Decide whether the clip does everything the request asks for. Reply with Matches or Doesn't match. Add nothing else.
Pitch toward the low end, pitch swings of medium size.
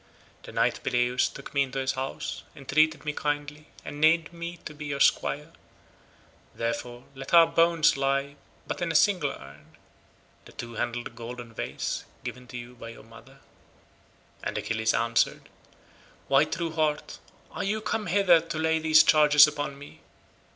Doesn't match